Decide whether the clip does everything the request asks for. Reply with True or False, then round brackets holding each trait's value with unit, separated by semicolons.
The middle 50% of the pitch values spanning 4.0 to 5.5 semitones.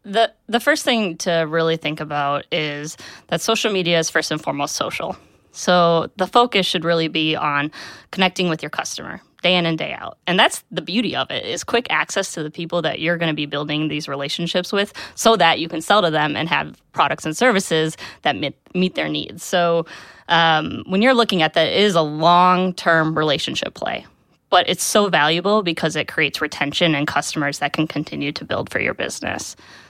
False (3.5 semitones)